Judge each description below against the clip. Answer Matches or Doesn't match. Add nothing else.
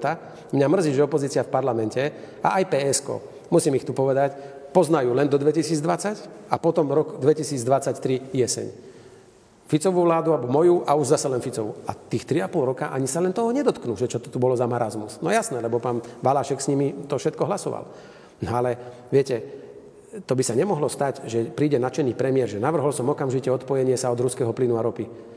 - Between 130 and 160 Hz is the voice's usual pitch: Matches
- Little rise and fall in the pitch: Doesn't match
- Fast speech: Matches